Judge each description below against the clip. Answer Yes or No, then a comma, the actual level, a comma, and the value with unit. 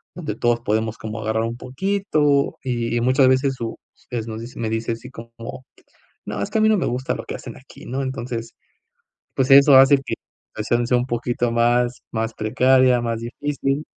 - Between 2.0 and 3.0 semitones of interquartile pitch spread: Yes, narrow, 2.5 semitones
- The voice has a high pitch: No, low, 120 Hz